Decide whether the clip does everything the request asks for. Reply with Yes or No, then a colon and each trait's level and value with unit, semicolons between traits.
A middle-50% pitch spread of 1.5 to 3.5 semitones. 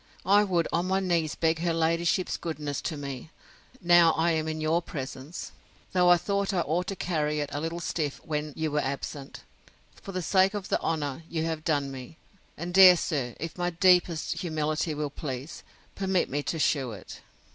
Yes: average, 3.0 semitones